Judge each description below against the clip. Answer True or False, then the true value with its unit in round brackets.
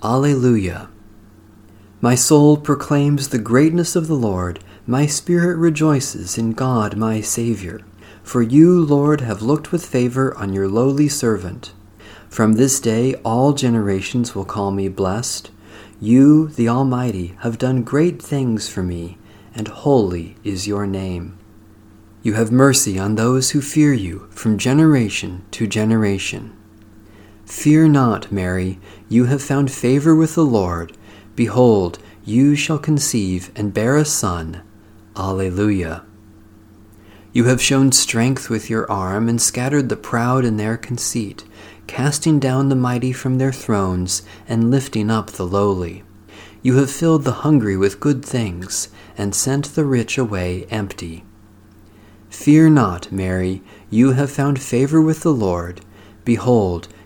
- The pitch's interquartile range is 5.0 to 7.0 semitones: False (4.5 semitones)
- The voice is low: True (110 Hz)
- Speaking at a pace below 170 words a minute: True (140 wpm)